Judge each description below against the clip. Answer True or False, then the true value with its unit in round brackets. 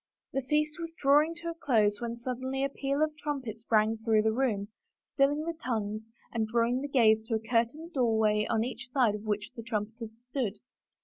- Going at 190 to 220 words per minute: True (195 wpm)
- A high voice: True (235 Hz)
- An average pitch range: True (4.2 semitones)